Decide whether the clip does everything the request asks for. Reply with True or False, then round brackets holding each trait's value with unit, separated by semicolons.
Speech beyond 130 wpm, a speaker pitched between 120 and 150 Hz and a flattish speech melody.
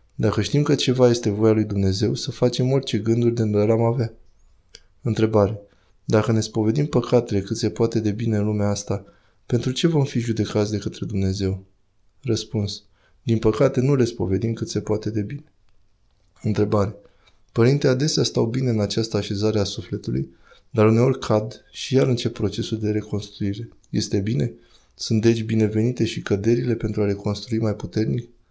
False (165 wpm; 110 Hz; 2.3 semitones)